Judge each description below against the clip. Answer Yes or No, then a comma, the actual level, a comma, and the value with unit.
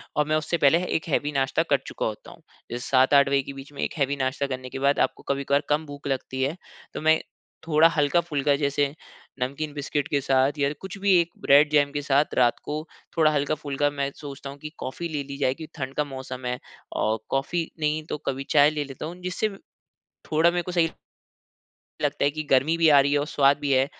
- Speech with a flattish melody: Yes, narrow, 2.0 semitones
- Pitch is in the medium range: Yes, medium, 145 Hz